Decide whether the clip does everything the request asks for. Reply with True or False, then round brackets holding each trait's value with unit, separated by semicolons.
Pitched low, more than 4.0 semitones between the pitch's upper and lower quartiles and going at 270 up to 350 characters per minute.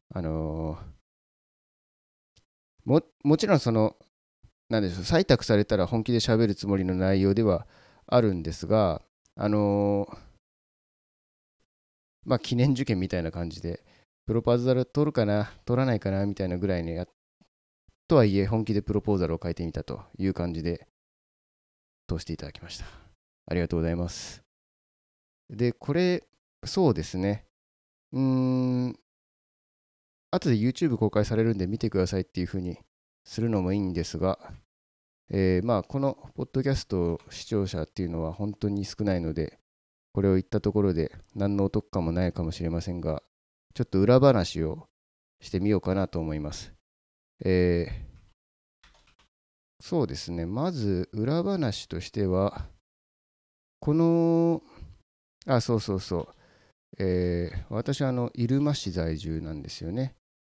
True (95 Hz; 5.6 semitones; 280 characters per minute)